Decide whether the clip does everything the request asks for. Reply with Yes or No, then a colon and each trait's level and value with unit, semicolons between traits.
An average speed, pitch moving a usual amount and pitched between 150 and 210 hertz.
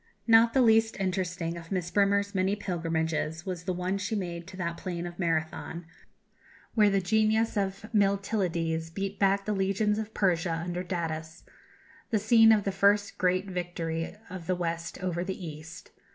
Yes: average, 165 wpm; average, 3.0 semitones; medium, 185 Hz